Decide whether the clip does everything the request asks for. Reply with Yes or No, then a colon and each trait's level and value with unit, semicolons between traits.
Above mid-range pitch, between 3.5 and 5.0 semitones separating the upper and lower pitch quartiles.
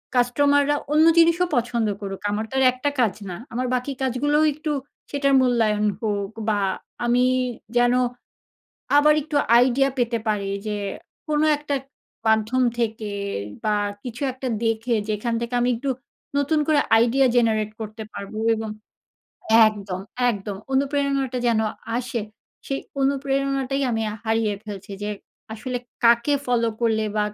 Yes: high, 240 Hz; average, 3.9 semitones